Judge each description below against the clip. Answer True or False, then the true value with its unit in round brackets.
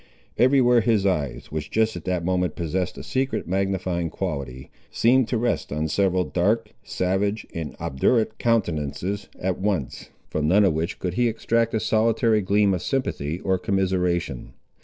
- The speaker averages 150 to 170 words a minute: True (160 wpm)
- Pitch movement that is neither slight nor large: True (4.4 semitones)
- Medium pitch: False (95 Hz)